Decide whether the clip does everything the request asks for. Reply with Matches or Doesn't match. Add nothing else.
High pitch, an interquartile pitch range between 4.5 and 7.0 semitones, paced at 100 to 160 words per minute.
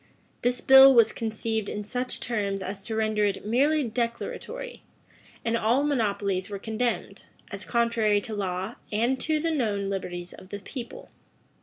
Doesn't match